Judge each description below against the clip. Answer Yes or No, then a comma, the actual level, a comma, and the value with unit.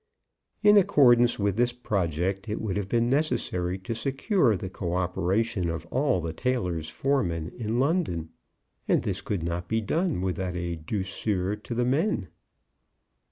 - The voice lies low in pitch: Yes, low, 100 Hz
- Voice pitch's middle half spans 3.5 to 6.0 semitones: Yes, wide, 5.6 semitones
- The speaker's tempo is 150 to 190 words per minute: Yes, average, 155 wpm